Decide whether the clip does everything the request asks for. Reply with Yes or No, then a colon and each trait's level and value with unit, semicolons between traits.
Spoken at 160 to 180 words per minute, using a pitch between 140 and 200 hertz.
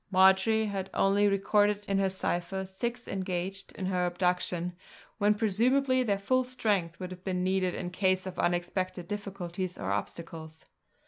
No: average, 150 wpm; high, 190 Hz